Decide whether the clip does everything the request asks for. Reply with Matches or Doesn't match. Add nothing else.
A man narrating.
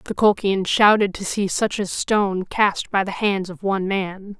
Doesn't match